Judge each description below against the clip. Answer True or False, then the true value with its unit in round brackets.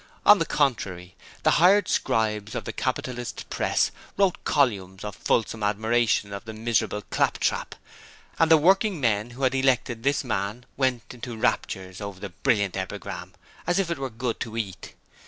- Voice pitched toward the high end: False (115 Hz)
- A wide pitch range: False (4.9 semitones)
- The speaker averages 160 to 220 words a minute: True (165 wpm)